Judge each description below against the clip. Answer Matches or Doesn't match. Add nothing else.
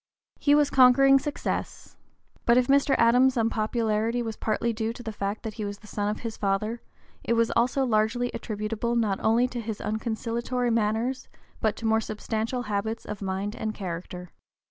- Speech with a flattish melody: Matches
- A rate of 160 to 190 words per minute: Matches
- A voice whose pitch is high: Matches